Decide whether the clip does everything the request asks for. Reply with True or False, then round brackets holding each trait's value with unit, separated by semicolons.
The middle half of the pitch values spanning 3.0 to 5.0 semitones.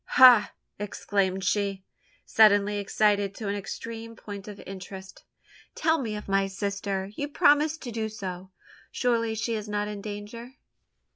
False (2.5 semitones)